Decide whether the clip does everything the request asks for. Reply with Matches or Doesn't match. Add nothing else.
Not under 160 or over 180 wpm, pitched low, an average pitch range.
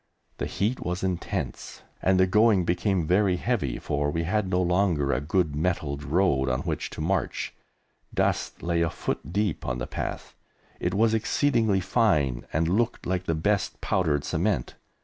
Matches